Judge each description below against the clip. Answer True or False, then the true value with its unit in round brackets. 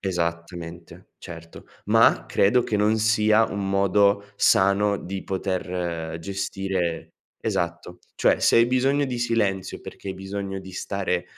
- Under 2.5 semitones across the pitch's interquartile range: False (2.8 semitones)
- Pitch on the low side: True (95 Hz)